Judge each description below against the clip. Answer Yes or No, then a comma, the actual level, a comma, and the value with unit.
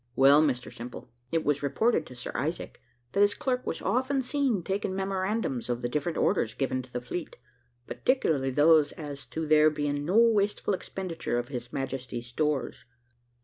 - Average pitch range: No, wide, 6.7 semitones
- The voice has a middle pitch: Yes, medium, 150 Hz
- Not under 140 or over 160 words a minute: No, average, 170 wpm